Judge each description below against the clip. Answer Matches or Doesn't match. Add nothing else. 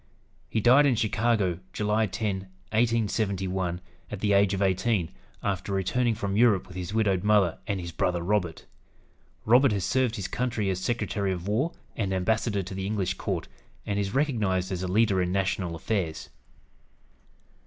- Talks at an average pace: Matches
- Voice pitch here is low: Matches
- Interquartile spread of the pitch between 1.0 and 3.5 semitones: Matches